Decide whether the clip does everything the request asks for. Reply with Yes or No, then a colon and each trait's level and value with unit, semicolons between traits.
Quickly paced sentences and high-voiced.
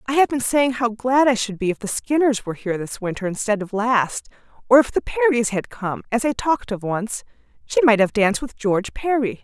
Yes: fast, 235 wpm; high, 230 Hz